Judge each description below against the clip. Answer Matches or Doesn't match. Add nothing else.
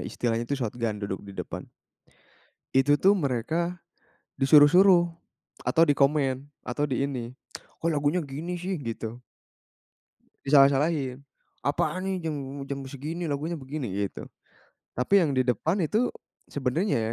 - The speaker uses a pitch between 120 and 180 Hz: Matches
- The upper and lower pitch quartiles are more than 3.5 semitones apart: Matches